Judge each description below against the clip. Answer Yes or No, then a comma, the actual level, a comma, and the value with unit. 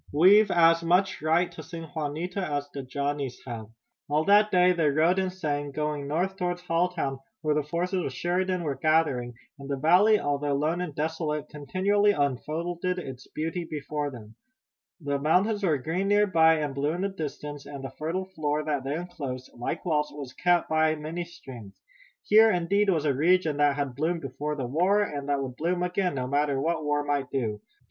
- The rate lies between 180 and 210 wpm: Yes, average, 190 wpm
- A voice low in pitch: No, medium, 155 Hz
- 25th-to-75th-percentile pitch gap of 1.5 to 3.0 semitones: No, average, 3.8 semitones